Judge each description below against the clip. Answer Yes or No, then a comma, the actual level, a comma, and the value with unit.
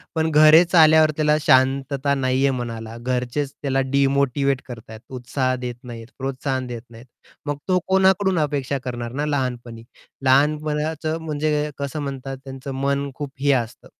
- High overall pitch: No, medium, 140 Hz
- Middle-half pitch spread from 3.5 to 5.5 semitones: No, average, 2.8 semitones